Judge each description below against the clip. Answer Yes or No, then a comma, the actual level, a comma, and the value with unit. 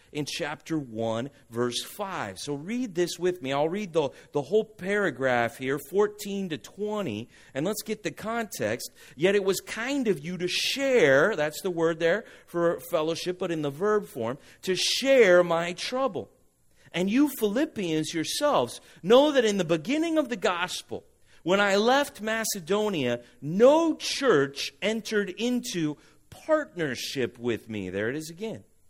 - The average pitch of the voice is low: No, medium, 180 Hz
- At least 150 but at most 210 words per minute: Yes, average, 155 wpm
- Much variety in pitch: Yes, wide, 6.4 semitones